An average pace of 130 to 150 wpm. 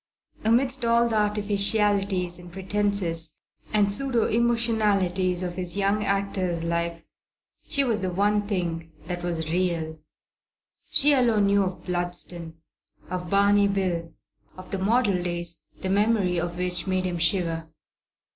Yes: slow, 135 wpm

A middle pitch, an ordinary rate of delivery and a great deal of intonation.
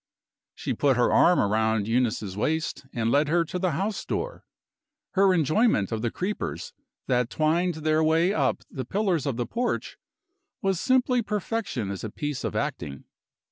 Yes: medium, 155 Hz; average, 165 wpm; wide, 7.9 semitones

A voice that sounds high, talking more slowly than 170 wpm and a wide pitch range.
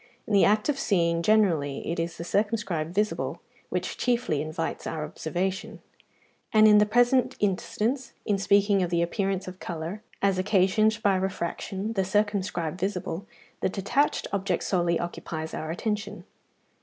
No: high, 195 Hz; average, 150 wpm; average, 3.6 semitones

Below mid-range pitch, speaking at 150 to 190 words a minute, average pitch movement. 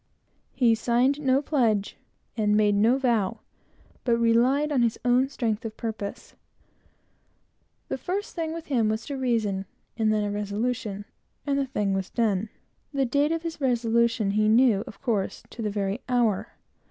No: high, 230 Hz; average, 165 wpm; average, 3.8 semitones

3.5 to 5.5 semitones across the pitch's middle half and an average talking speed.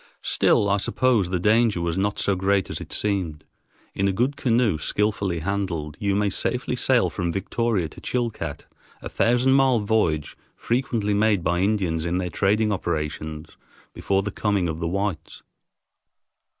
Yes: average, 4.0 semitones; average, 160 wpm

